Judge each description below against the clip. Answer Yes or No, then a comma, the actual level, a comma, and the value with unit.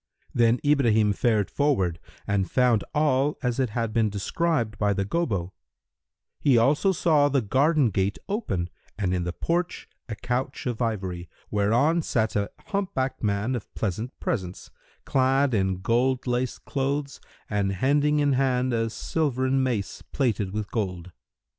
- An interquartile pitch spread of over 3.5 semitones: Yes, average, 5.2 semitones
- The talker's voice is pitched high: No, low, 120 Hz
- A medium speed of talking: Yes, average, 150 wpm